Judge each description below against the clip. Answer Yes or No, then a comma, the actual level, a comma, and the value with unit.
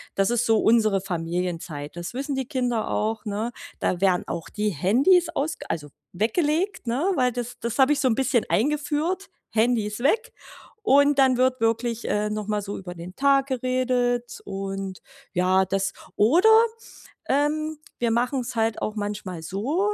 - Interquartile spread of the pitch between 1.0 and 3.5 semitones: No, wide, 5.5 semitones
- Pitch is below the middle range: No, high, 235 Hz